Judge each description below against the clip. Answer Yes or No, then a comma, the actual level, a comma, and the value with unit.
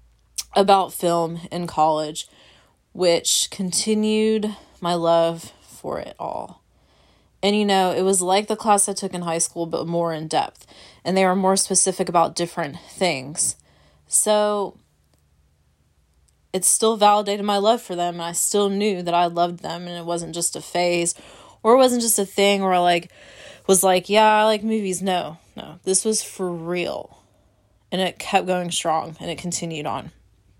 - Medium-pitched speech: Yes, medium, 175 Hz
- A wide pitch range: No, average, 3.3 semitones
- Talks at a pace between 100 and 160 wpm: No, average, 175 wpm